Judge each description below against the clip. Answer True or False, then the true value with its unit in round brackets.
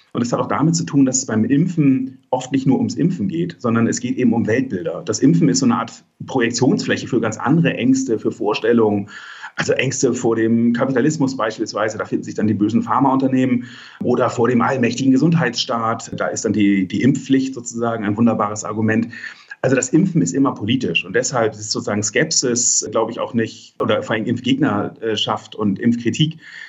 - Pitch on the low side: True (120 Hz)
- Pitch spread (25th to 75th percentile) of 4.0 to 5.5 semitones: False (3.5 semitones)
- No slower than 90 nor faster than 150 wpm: False (190 wpm)